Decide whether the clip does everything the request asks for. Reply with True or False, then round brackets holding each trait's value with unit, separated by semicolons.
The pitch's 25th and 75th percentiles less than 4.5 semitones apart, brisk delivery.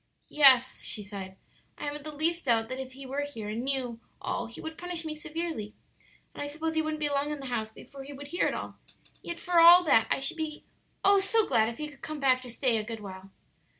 False (5.0 semitones; 250 wpm)